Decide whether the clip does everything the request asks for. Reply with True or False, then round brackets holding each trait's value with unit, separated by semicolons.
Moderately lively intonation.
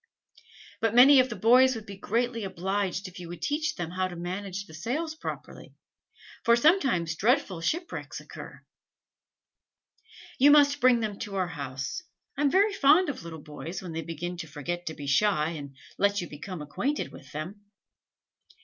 False (7.2 semitones)